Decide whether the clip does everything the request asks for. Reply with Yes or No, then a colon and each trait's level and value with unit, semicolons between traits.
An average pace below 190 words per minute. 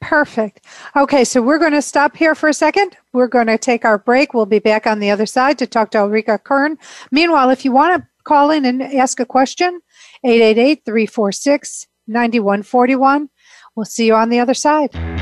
No: average, 195 wpm